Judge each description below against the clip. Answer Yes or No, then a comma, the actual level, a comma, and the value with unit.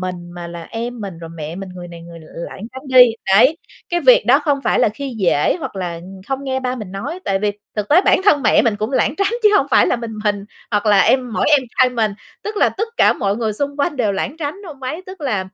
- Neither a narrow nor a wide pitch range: No, wide, 6.3 semitones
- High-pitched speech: Yes, high, 230 Hz